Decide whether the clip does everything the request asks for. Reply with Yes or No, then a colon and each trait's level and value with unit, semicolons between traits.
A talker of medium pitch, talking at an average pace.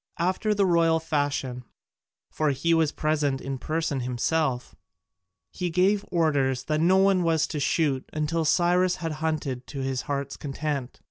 Yes: medium, 155 Hz; average, 150 wpm